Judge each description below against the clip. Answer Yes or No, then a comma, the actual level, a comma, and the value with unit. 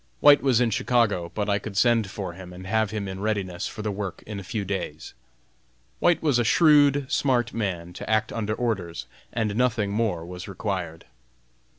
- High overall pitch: No, low, 105 Hz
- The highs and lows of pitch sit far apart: No, average, 3.8 semitones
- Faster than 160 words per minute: Yes, average, 190 wpm